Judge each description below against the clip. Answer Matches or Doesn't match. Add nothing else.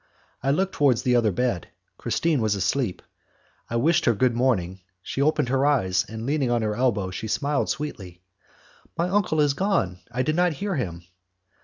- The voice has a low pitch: Matches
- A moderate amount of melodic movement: Doesn't match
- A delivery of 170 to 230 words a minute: Matches